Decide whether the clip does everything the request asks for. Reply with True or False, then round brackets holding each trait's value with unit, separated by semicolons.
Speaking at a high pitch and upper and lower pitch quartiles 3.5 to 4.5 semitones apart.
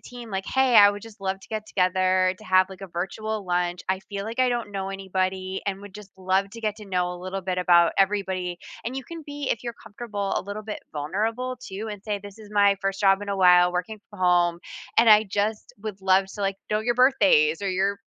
False (195 Hz; 2.5 semitones)